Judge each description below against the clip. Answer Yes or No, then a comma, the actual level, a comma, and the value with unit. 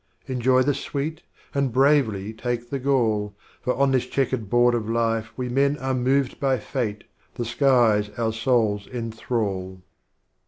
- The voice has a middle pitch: No, low, 120 Hz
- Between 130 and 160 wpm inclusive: Yes, average, 150 wpm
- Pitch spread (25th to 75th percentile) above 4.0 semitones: No, average, 3.1 semitones